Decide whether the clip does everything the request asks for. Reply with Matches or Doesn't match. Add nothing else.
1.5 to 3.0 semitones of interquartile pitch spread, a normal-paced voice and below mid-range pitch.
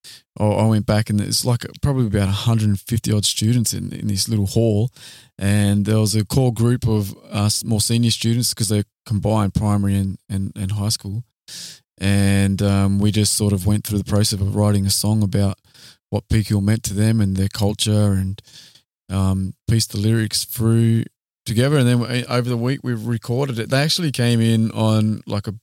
Matches